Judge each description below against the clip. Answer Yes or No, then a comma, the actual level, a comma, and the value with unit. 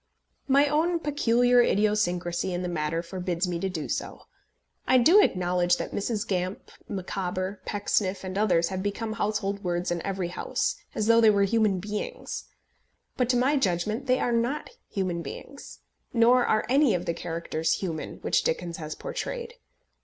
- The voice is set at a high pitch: Yes, high, 200 Hz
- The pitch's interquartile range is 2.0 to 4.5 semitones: No, average, 4.9 semitones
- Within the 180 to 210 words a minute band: No, average, 165 wpm